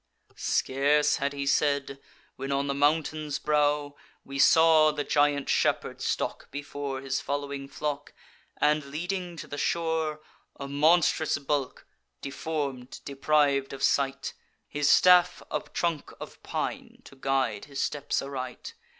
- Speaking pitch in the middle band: Yes, medium, 145 Hz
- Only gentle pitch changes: Yes, narrow, 1.7 semitones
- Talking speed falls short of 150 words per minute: Yes, slow, 135 wpm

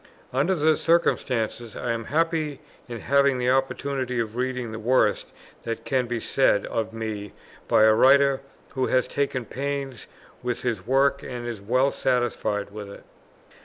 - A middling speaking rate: Yes, average, 160 wpm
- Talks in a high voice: No, low, 125 Hz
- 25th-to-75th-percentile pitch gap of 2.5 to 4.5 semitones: Yes, average, 3.3 semitones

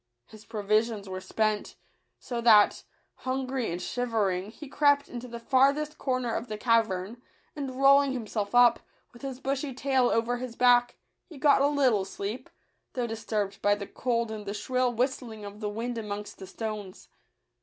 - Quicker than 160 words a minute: Yes, average, 175 wpm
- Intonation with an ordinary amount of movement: Yes, average, 3.6 semitones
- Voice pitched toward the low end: No, high, 235 Hz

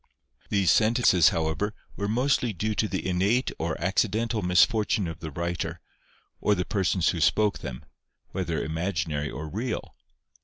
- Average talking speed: Yes, average, 145 wpm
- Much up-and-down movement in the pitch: No, average, 4.5 semitones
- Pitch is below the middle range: Yes, very low, 95 Hz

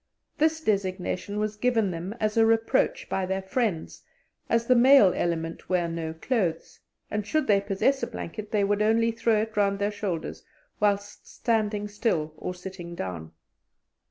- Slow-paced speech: No, average, 160 wpm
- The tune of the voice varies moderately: Yes, average, 3.5 semitones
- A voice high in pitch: Yes, high, 205 Hz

